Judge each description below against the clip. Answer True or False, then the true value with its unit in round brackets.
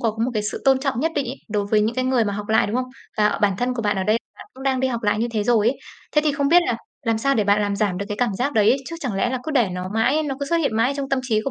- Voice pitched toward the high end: True (235 Hz)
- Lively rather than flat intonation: False (4.3 semitones)